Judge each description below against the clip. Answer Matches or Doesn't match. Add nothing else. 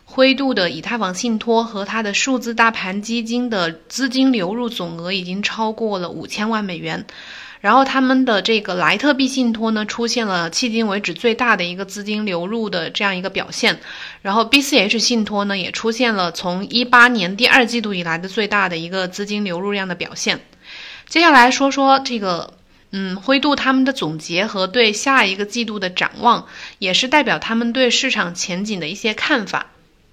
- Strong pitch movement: Doesn't match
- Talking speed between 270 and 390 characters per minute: Matches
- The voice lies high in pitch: Matches